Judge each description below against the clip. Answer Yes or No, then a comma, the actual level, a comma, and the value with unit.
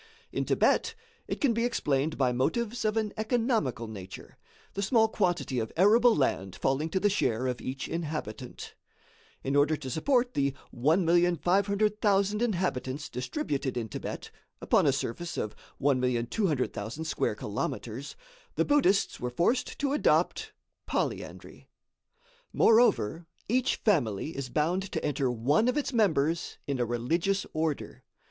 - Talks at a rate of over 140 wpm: No, slow, 135 wpm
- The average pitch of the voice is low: No, medium, 160 Hz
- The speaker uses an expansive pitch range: Yes, wide, 8.4 semitones